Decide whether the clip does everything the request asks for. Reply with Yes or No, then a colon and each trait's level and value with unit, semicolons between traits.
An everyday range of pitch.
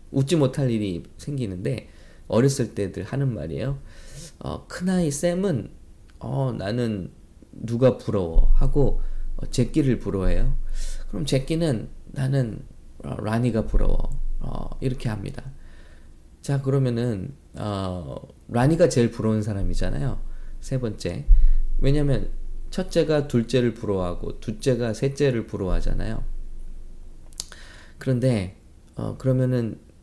No: wide, 6.6 semitones